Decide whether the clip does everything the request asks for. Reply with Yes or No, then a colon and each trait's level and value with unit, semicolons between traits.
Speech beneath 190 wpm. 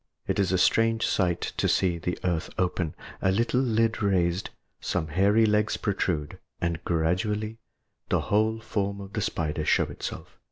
Yes: average, 160 wpm